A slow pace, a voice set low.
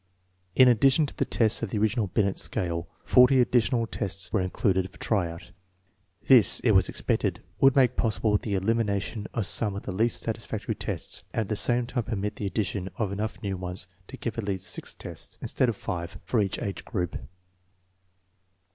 No: average, 190 wpm; low, 105 Hz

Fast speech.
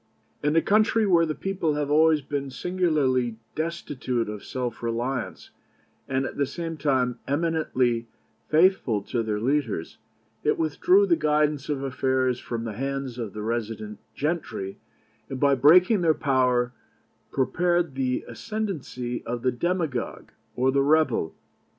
No: average, 140 wpm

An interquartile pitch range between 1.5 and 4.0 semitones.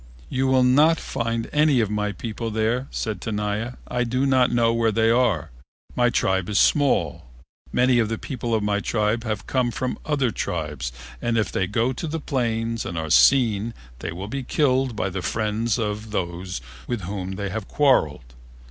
Yes: average, 3.4 semitones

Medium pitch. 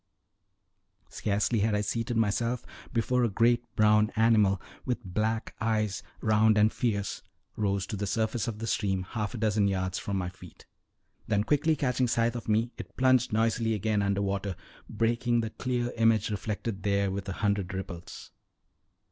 No: low, 110 Hz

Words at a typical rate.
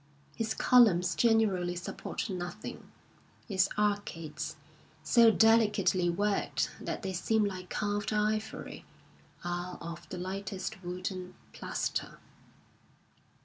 No: slow, 105 wpm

